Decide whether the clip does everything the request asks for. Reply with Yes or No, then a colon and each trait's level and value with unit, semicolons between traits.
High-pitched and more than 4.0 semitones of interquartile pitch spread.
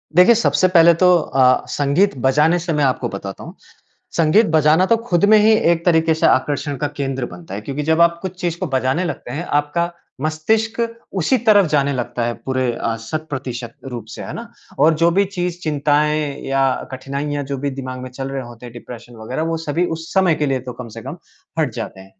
No: medium, 150 Hz; average, 4.7 semitones